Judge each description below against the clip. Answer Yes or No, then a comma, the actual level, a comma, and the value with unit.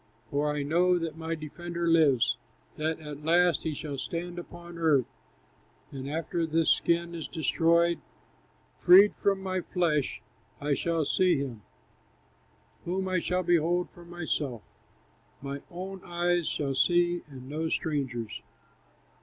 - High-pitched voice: No, medium, 165 Hz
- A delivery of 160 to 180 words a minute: No, slow, 135 wpm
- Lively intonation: No, average, 2.9 semitones